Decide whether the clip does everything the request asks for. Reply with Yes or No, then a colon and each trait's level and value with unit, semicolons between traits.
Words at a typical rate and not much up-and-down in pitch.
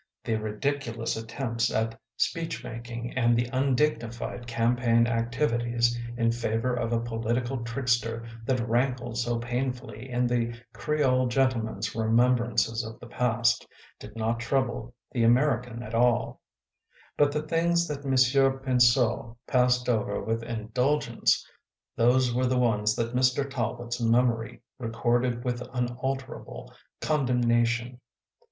No: slow, 130 wpm; narrow, 1.7 semitones